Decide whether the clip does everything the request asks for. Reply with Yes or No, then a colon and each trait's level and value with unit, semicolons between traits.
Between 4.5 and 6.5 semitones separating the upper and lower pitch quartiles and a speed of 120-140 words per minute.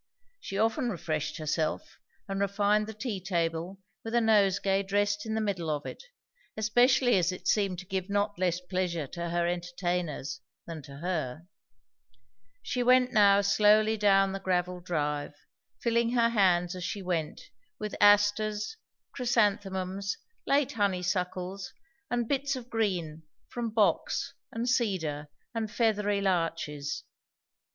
No: average, 3.8 semitones; slow, 135 wpm